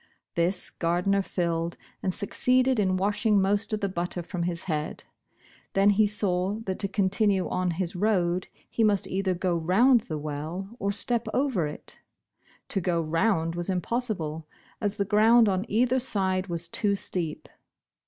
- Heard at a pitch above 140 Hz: Yes, high, 190 Hz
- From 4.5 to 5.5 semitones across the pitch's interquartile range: No, average, 3.3 semitones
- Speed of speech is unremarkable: Yes, average, 160 wpm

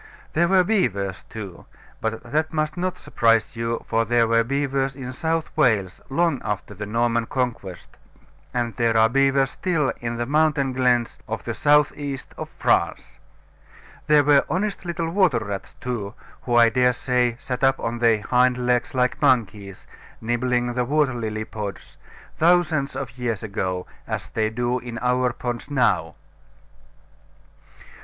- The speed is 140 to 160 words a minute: Yes, average, 155 wpm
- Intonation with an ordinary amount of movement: Yes, average, 3.4 semitones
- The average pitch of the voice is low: Yes, low, 125 Hz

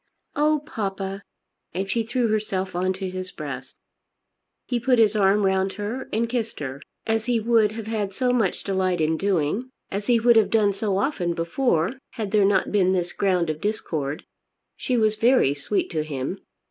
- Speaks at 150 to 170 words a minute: No, average, 185 wpm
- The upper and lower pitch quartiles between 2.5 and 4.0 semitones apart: Yes, average, 3.7 semitones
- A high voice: Yes, high, 200 Hz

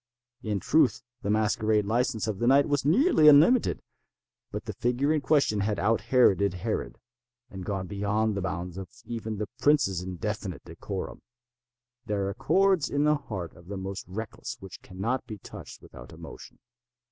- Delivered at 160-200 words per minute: Yes, average, 165 wpm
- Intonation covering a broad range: Yes, wide, 5.8 semitones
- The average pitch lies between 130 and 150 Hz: No, low, 110 Hz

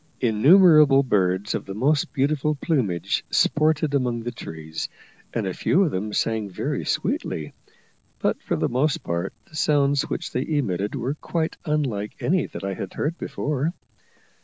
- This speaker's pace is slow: No, average, 160 wpm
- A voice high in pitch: No, low, 135 Hz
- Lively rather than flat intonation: Yes, wide, 6.6 semitones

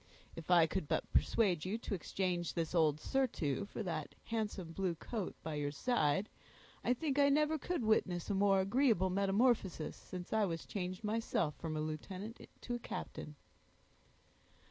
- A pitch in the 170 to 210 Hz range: Yes, high, 190 Hz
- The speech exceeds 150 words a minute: Yes, average, 165 wpm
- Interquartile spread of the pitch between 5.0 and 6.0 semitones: Yes, average, 5.3 semitones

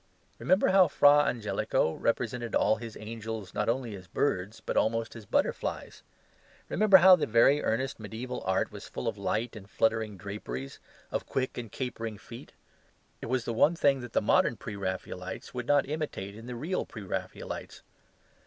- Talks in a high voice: No, low, 115 Hz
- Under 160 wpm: No, average, 170 wpm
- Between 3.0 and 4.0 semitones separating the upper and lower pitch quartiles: Yes, average, 3.7 semitones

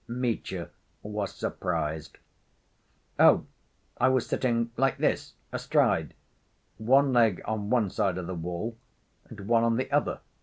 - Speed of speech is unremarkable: No, slow, 130 wpm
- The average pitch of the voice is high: No, low, 115 Hz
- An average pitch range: Yes, average, 4.3 semitones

